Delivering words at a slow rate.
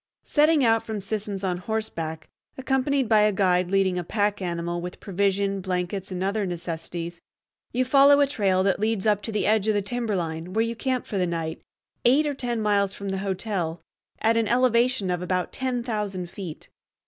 No: average, 190 wpm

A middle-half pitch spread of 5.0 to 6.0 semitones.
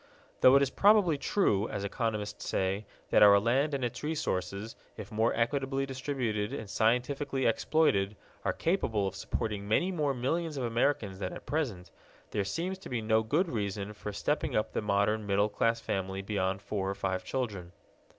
Yes: average, 5.3 semitones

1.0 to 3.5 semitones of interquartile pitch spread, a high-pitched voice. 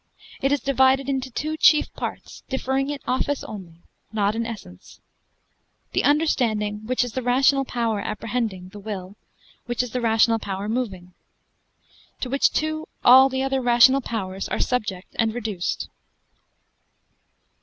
No: average, 4.1 semitones; high, 240 Hz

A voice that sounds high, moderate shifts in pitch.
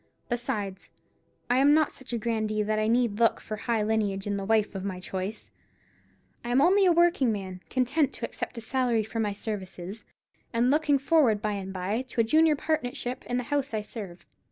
Yes: high, 230 Hz; average, 3.9 semitones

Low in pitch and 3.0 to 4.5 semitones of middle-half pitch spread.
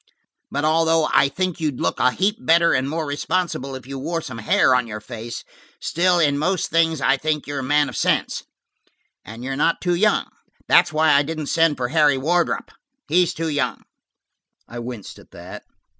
No: medium, 150 Hz; average, 3.8 semitones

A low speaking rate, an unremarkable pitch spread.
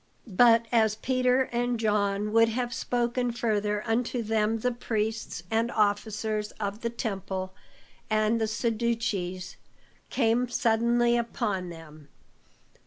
No: slow, 115 wpm; narrow, 2.2 semitones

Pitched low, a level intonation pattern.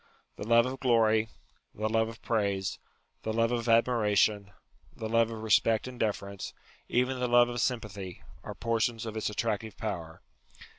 Yes: low, 110 Hz; narrow, 1.8 semitones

